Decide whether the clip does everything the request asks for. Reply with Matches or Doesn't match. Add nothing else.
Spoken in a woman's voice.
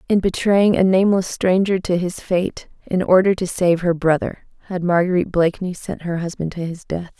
Matches